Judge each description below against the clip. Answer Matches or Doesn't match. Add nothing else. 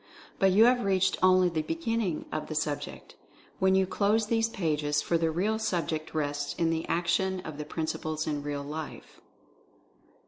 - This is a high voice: Doesn't match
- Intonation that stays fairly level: Doesn't match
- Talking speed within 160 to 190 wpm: Matches